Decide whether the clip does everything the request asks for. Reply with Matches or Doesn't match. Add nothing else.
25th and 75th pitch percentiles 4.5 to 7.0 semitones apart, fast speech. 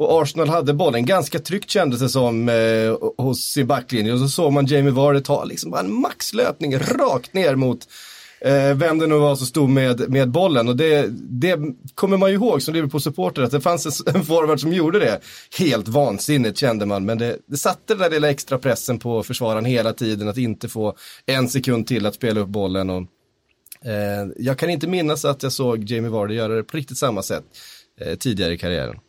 Matches